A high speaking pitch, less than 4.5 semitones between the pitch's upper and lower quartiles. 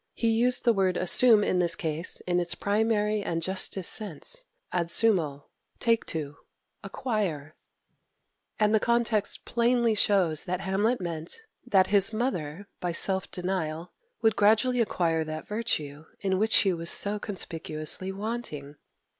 No: high, 195 Hz; average, 4.8 semitones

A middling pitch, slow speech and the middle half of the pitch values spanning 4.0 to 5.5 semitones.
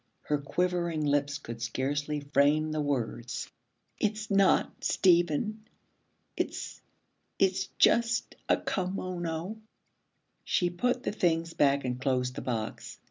Yes: medium, 155 Hz; slow, 115 wpm; average, 4.7 semitones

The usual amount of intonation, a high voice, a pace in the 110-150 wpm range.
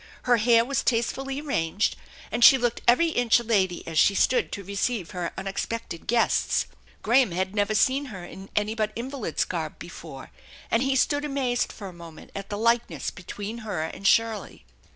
No: average, 4.3 semitones; high, 220 Hz; average, 180 wpm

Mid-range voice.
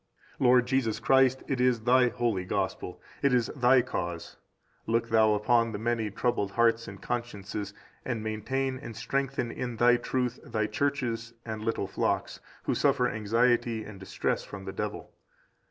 No: low, 115 Hz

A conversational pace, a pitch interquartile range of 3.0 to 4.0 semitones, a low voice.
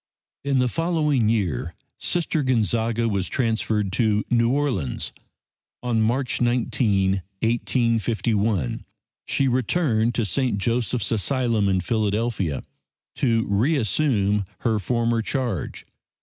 No: slow, 105 wpm; average, 3.5 semitones; low, 115 Hz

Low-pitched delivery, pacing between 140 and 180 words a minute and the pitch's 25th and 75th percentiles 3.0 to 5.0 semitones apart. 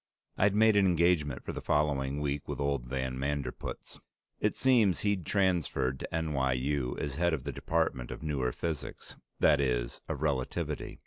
Yes: very low, 75 Hz; average, 165 wpm; average, 4.2 semitones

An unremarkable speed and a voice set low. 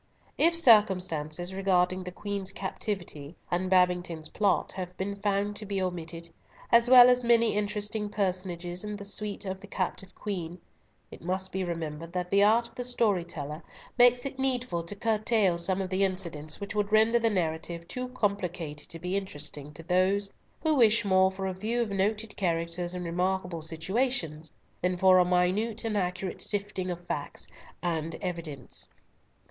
No: average, 170 wpm; high, 190 Hz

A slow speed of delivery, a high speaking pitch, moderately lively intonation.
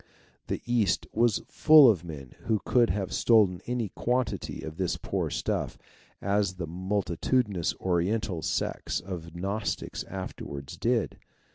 No: slow, 130 wpm; very low, 95 Hz; average, 4.7 semitones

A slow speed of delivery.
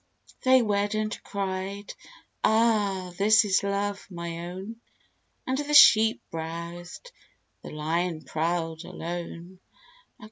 Yes: slow, 105 wpm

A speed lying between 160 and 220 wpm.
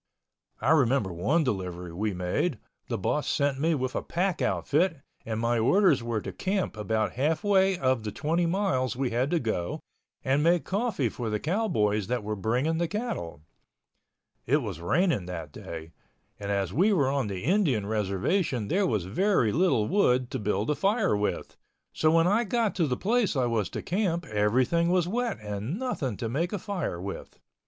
Yes: average, 185 wpm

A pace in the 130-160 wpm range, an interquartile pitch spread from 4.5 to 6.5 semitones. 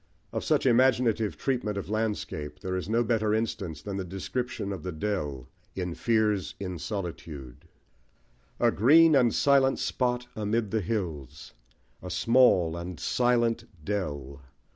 Yes: average, 140 wpm; average, 5.2 semitones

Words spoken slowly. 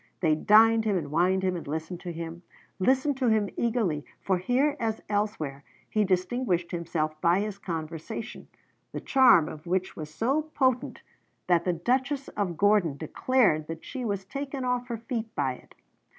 No: average, 170 wpm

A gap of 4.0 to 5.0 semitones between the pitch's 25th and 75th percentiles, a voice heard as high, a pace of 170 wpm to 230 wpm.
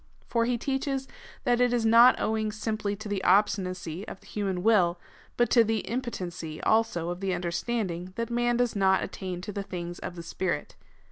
Yes: average, 4.4 semitones; high, 205 Hz; average, 190 wpm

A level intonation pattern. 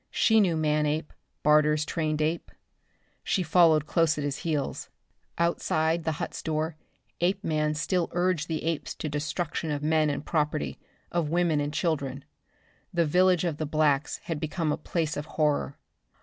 Yes: narrow, 2.1 semitones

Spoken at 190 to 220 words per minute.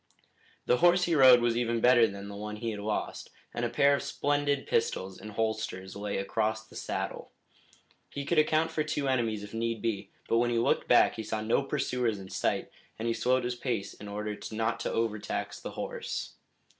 Yes: fast, 205 wpm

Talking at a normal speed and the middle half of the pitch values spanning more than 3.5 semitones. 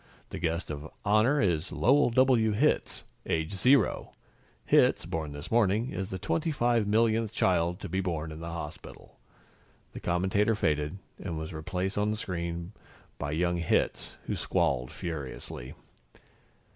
Yes: average, 145 wpm; average, 5.2 semitones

